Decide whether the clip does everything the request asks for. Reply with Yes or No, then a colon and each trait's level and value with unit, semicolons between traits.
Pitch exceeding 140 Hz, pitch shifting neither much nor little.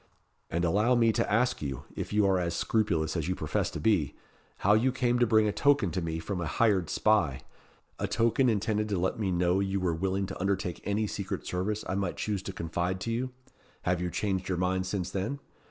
No: very low, 95 Hz; average, 3.4 semitones